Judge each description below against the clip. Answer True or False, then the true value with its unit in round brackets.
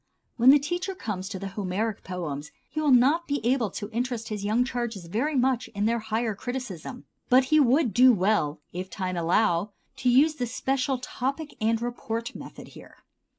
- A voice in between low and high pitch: False (235 Hz)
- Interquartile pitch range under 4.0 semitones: False (4.5 semitones)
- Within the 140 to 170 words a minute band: False (185 wpm)